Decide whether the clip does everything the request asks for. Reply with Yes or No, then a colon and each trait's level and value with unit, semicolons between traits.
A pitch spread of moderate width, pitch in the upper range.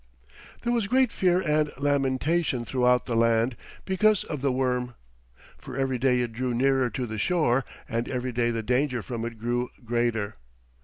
No: average, 3.2 semitones; low, 125 Hz